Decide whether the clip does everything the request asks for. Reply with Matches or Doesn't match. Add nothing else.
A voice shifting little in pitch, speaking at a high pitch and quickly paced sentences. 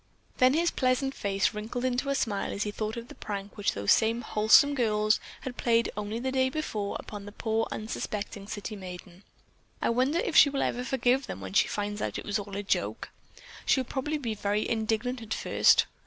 Doesn't match